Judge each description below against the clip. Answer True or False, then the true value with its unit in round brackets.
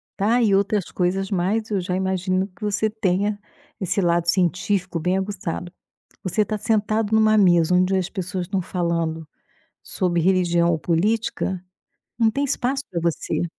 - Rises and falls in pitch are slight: False (3.1 semitones)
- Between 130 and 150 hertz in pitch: False (190 Hz)